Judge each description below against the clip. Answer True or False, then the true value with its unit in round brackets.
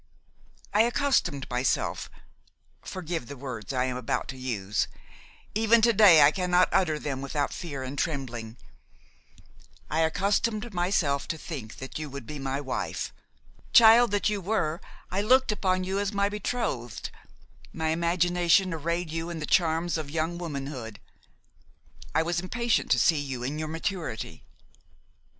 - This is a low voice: False (165 Hz)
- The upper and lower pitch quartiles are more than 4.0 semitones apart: True (5.6 semitones)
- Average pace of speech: True (145 wpm)